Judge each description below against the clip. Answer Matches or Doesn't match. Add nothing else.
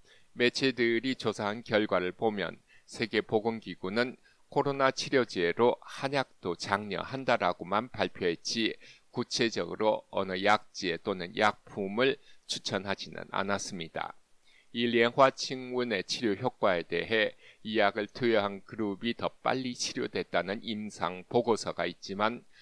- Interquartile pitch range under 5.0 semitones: Matches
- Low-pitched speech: Matches